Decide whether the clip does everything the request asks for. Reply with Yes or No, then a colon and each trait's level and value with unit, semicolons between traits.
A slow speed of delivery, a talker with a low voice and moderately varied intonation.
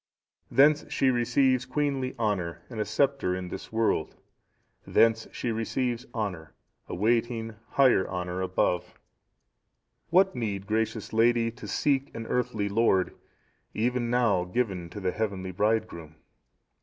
Yes: slow, 125 wpm; low, 115 Hz; average, 4.7 semitones